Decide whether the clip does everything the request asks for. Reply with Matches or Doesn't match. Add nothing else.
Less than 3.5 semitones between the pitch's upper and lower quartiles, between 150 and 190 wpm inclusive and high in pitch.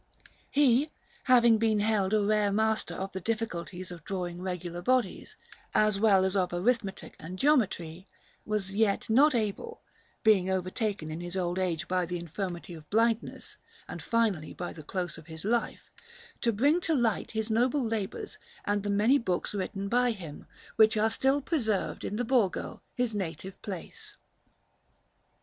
Doesn't match